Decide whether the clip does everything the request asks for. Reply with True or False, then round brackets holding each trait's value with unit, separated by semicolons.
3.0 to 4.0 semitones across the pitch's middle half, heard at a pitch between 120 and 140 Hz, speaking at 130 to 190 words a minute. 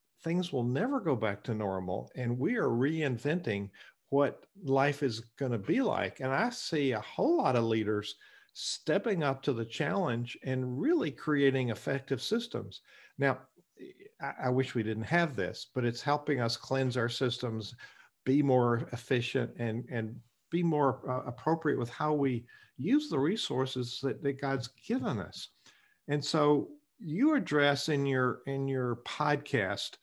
True (3.7 semitones; 135 Hz; 160 wpm)